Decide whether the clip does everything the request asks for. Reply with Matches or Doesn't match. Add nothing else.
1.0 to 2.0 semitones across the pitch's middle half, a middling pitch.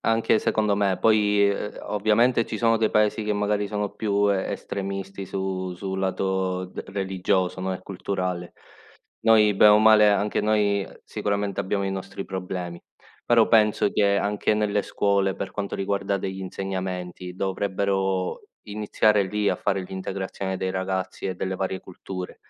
Doesn't match